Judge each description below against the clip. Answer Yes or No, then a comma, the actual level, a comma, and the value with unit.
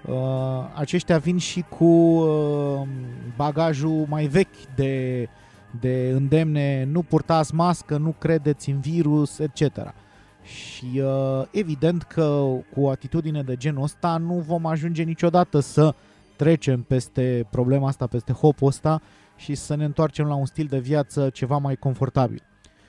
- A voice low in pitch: No, medium, 145 Hz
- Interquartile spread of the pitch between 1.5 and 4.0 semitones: Yes, average, 3.3 semitones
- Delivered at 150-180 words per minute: No, average, 140 wpm